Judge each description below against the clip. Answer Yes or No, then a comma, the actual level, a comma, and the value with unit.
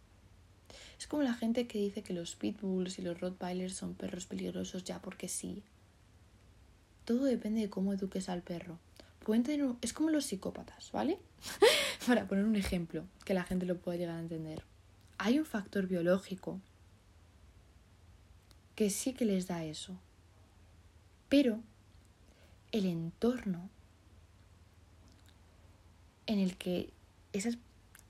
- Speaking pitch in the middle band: Yes, medium, 170 Hz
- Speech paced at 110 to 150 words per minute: Yes, average, 130 wpm